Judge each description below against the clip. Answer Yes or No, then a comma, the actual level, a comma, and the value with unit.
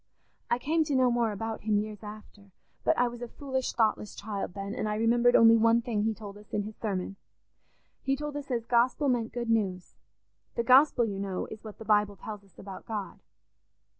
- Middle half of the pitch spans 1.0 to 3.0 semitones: Yes, narrow, 2.6 semitones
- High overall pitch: Yes, high, 225 Hz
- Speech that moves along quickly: Yes, fast, 210 wpm